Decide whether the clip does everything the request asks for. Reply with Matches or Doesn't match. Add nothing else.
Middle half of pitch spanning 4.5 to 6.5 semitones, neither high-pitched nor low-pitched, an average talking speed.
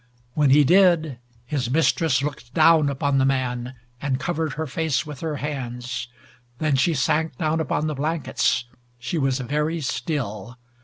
Doesn't match